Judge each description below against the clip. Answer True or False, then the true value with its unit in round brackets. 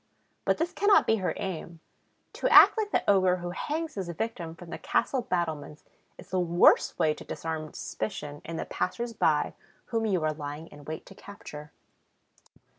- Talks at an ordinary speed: True (180 wpm)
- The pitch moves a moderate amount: False (5.9 semitones)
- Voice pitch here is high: False (175 Hz)